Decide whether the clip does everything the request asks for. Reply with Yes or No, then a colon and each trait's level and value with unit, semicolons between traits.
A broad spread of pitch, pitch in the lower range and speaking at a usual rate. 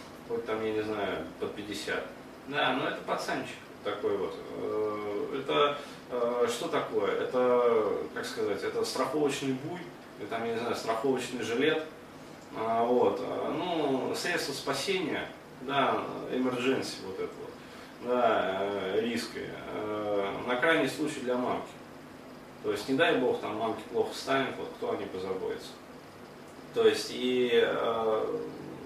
Yes: wide, 6.4 semitones; low, 125 Hz; average, 130 wpm